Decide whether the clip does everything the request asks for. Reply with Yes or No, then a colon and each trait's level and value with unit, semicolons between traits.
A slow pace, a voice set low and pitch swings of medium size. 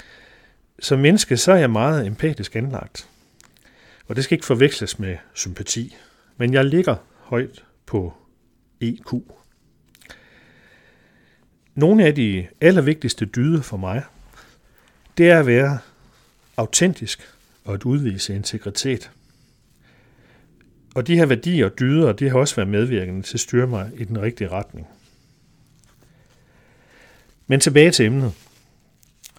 Yes: slow, 125 wpm; low, 125 Hz; average, 4.9 semitones